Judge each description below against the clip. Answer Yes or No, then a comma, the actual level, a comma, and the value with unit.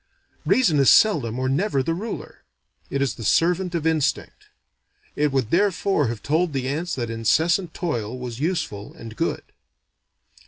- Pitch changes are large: Yes, wide, 5.8 semitones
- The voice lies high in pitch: No, medium, 145 Hz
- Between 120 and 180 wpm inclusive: Yes, average, 155 wpm